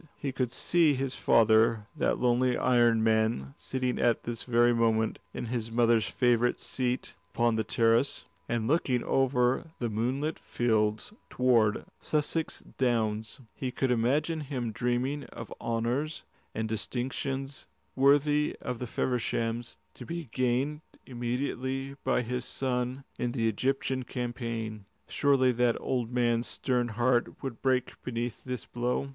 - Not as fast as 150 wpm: Yes, average, 140 wpm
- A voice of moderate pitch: No, low, 125 Hz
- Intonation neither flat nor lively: No, narrow, 2.3 semitones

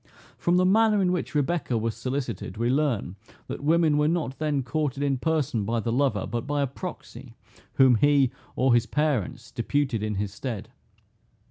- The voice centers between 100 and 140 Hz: Yes, low, 135 Hz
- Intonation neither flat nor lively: Yes, average, 4.5 semitones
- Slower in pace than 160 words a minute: No, average, 175 wpm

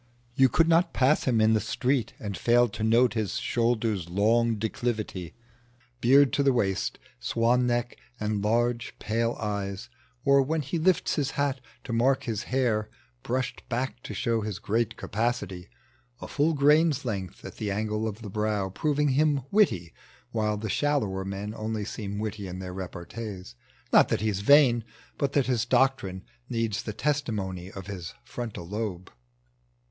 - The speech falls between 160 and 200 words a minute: Yes, average, 165 wpm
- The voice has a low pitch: Yes, low, 115 Hz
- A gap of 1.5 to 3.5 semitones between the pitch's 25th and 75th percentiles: No, average, 4.1 semitones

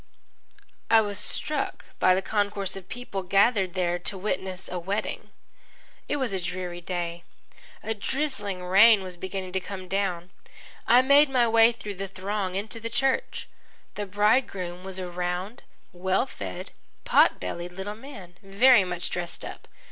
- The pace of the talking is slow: No, average, 155 wpm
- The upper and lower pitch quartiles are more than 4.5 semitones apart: No, average, 3.3 semitones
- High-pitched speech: Yes, high, 195 Hz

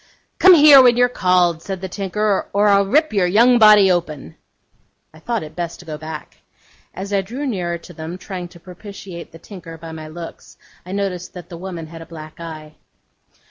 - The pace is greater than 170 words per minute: Yes, average, 200 wpm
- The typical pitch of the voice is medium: Yes, medium, 180 Hz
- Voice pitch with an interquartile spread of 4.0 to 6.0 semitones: No, average, 3.6 semitones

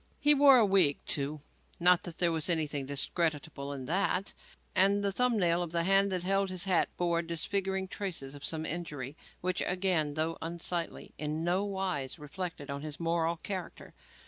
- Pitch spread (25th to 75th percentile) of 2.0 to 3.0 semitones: No, average, 3.7 semitones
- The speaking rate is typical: Yes, average, 175 wpm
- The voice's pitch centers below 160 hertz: No, medium, 170 Hz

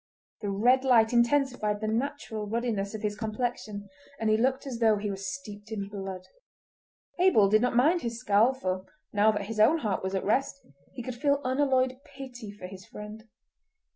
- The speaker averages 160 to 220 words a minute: Yes, average, 185 wpm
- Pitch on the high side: Yes, high, 220 Hz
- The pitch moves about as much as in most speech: Yes, average, 3.8 semitones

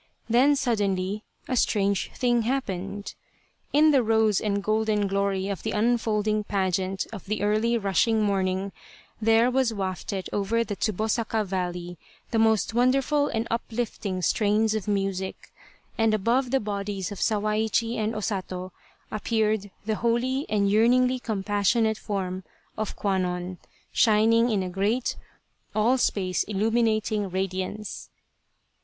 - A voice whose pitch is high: Yes, high, 215 Hz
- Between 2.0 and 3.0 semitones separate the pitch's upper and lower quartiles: Yes, narrow, 2.6 semitones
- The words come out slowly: Yes, slow, 130 wpm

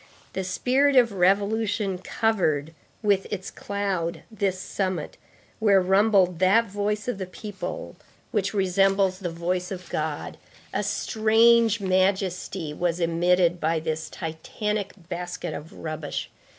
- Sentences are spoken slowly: Yes, slow, 125 wpm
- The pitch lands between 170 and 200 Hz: Yes, high, 190 Hz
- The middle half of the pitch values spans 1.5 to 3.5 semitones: Yes, average, 2.8 semitones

